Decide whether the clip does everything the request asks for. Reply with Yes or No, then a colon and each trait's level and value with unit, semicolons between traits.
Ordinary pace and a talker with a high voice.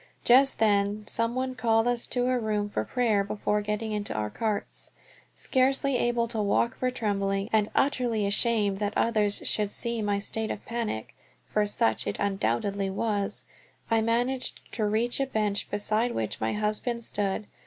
Yes: average, 165 wpm; high, 215 Hz